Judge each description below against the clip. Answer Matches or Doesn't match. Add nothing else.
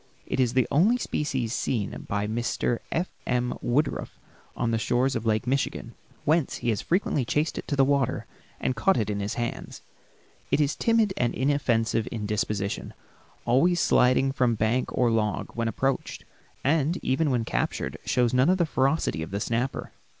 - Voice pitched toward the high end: Doesn't match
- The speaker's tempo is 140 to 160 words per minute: Doesn't match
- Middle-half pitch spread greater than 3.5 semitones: Matches